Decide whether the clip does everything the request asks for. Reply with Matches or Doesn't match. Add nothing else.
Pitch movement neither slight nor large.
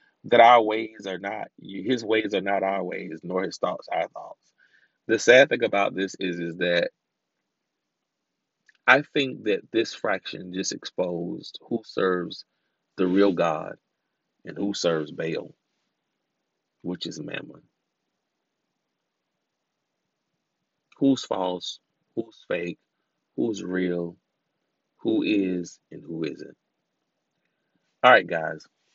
Doesn't match